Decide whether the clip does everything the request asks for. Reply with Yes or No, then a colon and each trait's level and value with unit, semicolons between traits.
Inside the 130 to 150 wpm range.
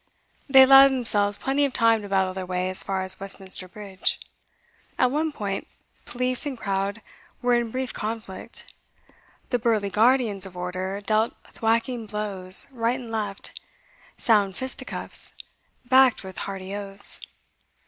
Yes: average, 140 wpm